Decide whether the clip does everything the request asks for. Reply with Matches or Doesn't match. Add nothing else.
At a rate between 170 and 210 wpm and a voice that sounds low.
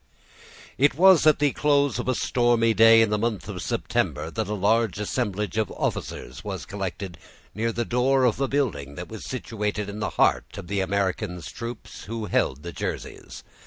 Matches